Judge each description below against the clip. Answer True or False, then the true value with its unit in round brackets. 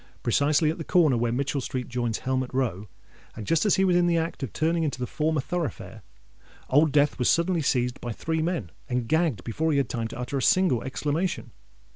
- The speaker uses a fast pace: True (215 wpm)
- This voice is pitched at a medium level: True (145 Hz)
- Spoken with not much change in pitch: False (4.7 semitones)